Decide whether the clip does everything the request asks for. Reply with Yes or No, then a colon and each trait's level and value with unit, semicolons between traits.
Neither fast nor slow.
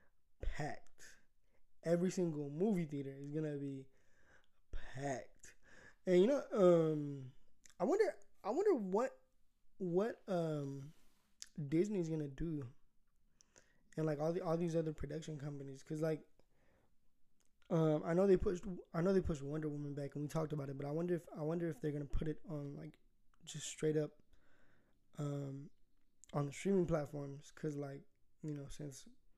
Yes: average, 155 wpm